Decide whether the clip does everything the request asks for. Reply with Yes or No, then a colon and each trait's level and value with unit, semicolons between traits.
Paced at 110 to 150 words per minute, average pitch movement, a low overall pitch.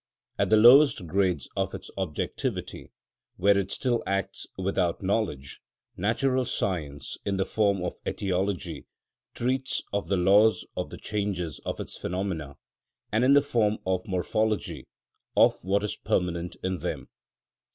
Yes: average, 140 wpm; average, 3.3 semitones; low, 100 Hz